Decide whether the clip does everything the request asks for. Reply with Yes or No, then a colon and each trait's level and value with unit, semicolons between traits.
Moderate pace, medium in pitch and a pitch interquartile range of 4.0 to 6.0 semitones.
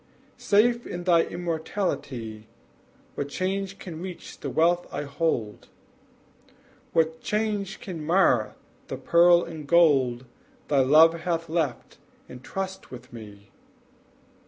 No: slow, 115 wpm; medium, 165 Hz; average, 5.2 semitones